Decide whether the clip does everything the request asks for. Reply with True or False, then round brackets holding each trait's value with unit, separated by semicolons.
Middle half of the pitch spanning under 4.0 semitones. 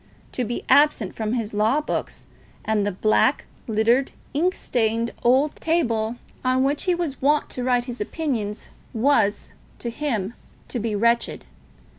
False (4.3 semitones)